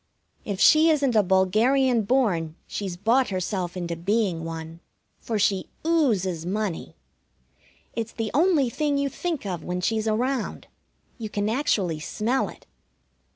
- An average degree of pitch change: No, wide, 6.2 semitones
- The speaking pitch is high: Yes, high, 215 Hz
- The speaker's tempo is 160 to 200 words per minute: No, average, 140 wpm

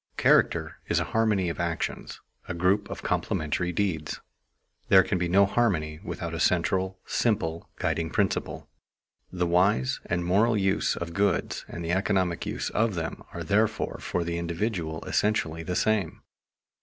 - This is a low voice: Yes, very low, 90 Hz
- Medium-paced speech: Yes, average, 155 wpm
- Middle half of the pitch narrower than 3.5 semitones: Yes, average, 3.0 semitones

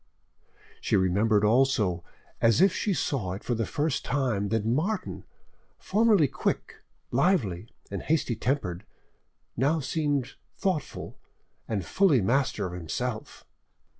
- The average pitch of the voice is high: No, low, 125 Hz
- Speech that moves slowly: Yes, slow, 120 wpm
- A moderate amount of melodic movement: No, wide, 6.7 semitones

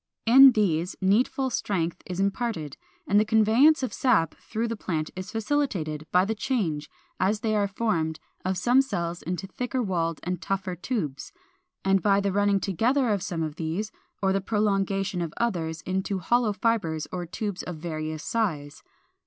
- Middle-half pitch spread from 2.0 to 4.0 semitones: No, average, 4.6 semitones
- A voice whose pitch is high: Yes, high, 195 Hz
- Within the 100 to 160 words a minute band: No, average, 170 wpm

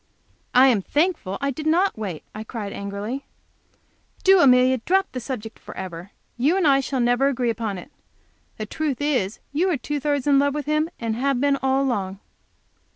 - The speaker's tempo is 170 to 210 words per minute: Yes, average, 185 wpm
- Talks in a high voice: Yes, very high, 265 Hz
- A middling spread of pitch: Yes, average, 4.8 semitones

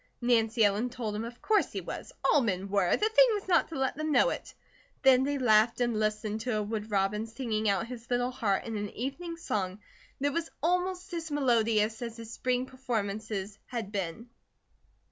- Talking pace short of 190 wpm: No, average, 195 wpm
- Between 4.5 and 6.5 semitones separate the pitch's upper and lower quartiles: No, average, 3.9 semitones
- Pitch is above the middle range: Yes, high, 230 Hz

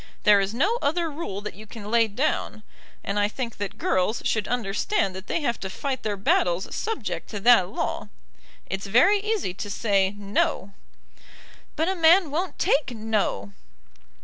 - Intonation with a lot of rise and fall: Yes, wide, 6.7 semitones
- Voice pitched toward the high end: Yes, high, 220 Hz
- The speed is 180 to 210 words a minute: No, average, 170 wpm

